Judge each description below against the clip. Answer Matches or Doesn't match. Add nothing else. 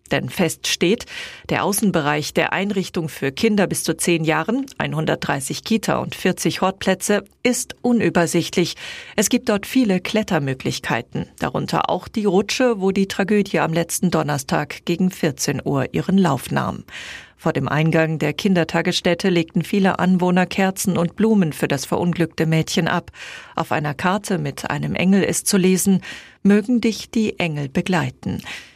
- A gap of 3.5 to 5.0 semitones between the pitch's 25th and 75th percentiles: Matches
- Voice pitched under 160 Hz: Doesn't match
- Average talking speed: Matches